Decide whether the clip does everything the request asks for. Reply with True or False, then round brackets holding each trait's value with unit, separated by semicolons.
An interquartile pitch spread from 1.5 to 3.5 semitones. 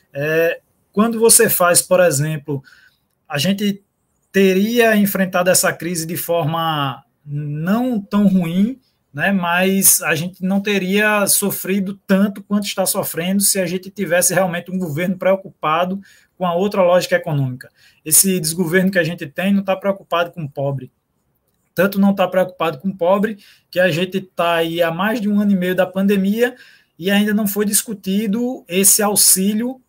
True (2.8 semitones)